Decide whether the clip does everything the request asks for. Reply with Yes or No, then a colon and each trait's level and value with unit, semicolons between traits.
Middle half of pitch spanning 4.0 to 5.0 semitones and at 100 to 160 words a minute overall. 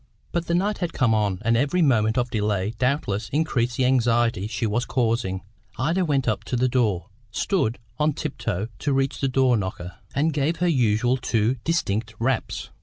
No: average, 4.4 semitones; average, 180 wpm